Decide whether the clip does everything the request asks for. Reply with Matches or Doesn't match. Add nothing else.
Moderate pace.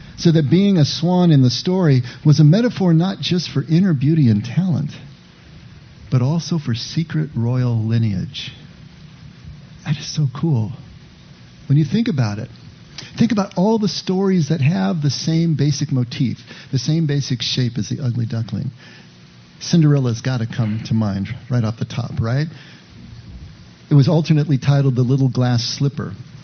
Matches